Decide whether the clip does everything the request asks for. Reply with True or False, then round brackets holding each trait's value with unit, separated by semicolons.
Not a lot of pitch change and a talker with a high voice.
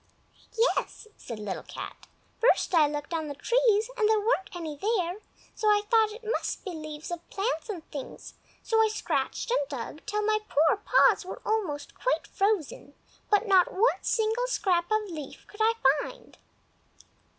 False (5.6 semitones; 410 Hz)